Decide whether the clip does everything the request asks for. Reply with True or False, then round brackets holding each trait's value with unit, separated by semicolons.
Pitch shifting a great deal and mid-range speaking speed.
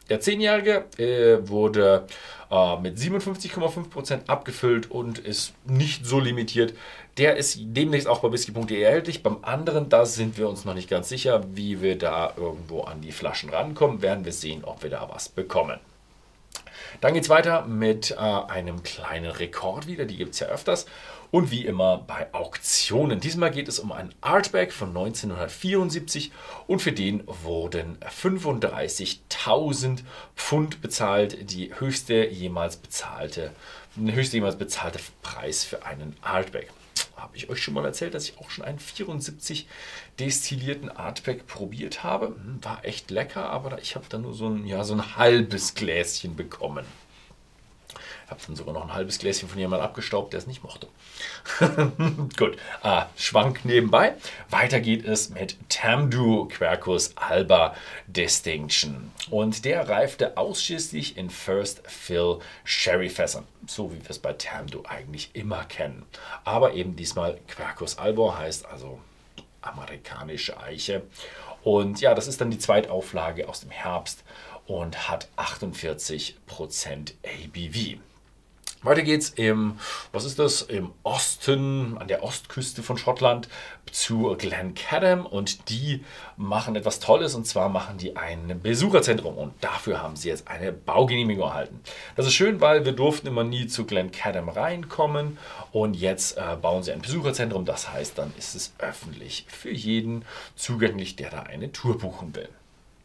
True (6.4 semitones; 150 wpm)